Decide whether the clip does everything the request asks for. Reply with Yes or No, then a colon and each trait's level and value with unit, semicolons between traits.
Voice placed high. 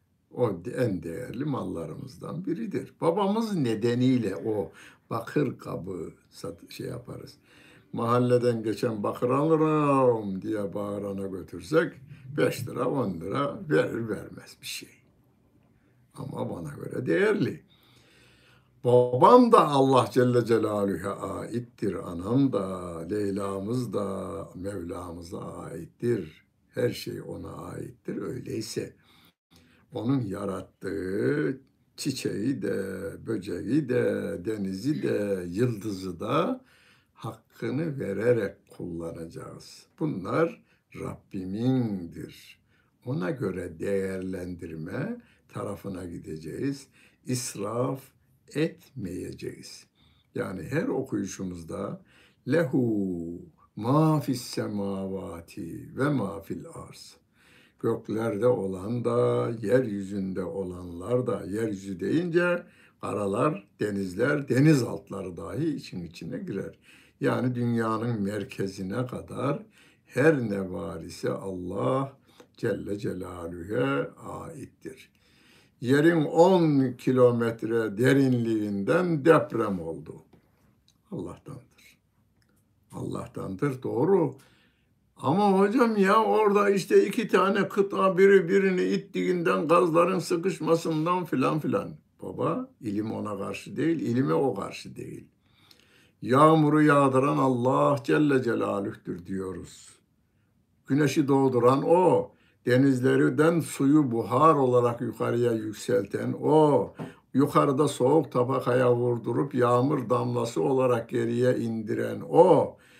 No: low, 120 Hz